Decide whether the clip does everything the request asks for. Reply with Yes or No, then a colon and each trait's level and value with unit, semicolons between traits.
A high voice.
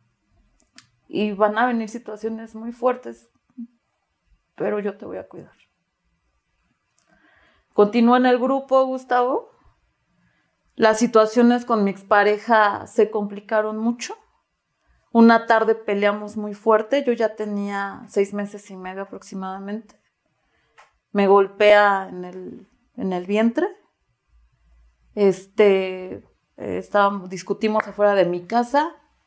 Yes: high, 215 Hz